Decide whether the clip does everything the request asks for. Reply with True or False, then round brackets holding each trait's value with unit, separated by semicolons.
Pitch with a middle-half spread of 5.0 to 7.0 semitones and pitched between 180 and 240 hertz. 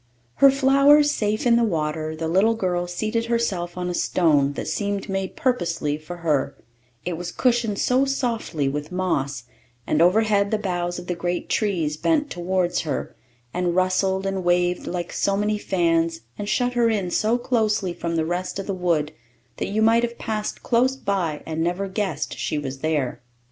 False (4.5 semitones; 185 Hz)